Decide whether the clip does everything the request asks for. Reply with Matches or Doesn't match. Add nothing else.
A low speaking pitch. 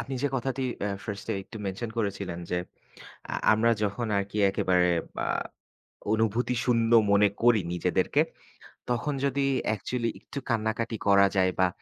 Matches